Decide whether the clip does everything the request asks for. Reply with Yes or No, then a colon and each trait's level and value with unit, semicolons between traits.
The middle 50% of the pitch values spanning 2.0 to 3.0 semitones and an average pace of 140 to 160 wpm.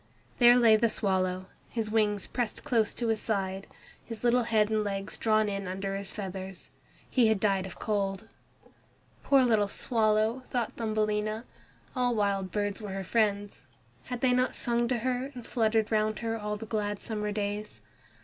No: narrow, 2.5 semitones; average, 175 wpm